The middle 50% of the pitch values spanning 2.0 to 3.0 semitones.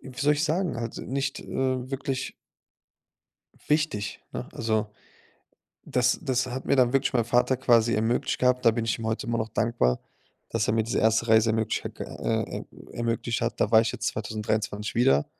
Yes: narrow, 2.5 semitones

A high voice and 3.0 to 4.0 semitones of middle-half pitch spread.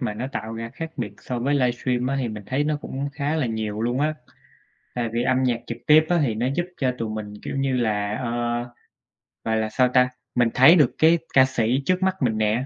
No: low, 125 Hz; average, 3.5 semitones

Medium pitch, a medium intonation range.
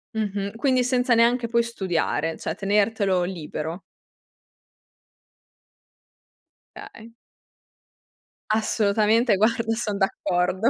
No: high, 215 Hz; average, 3.3 semitones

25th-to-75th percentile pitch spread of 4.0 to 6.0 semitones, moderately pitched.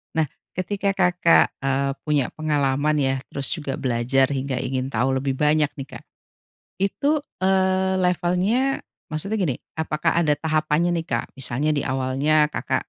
Yes: average, 4.8 semitones; medium, 150 Hz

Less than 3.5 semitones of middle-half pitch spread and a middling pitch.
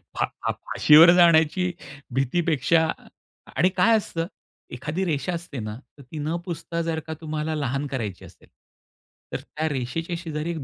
Yes: average, 2.9 semitones; medium, 160 Hz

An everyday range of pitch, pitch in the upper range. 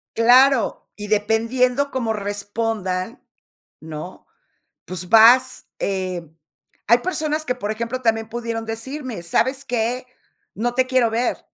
Yes: average, 3.5 semitones; high, 230 Hz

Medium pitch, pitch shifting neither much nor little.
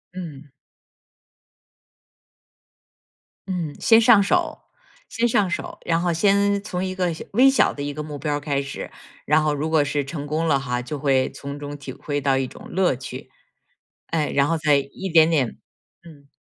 Yes: medium, 150 Hz; average, 4.1 semitones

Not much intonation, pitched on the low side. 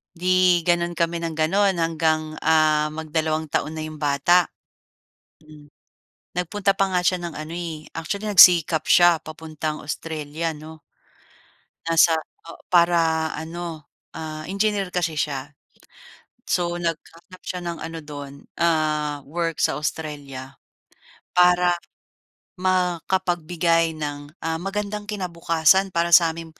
No: narrow, 2.1 semitones; medium, 165 Hz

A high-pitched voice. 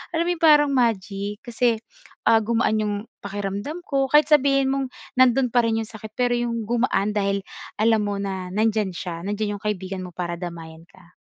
Yes: high, 215 Hz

